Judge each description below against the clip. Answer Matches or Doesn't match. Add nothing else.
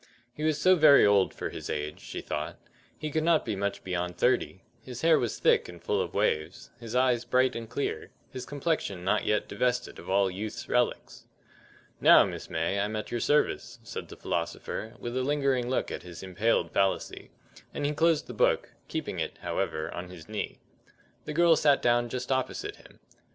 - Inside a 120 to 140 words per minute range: Doesn't match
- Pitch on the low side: Matches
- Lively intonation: Matches